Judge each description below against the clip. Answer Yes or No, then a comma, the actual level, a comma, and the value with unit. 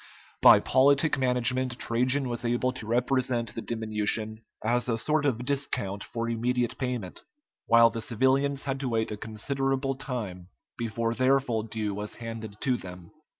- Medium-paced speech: Yes, average, 155 wpm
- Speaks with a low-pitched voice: Yes, low, 120 Hz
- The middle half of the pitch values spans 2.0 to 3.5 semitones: Yes, average, 2.8 semitones